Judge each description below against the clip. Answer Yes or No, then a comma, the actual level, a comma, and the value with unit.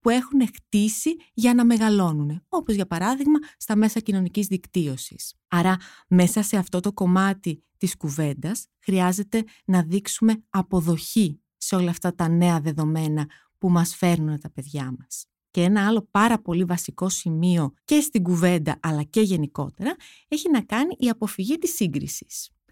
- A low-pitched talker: No, high, 190 Hz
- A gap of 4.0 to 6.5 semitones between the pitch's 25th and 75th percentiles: Yes, average, 4.6 semitones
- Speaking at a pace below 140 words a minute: No, average, 150 wpm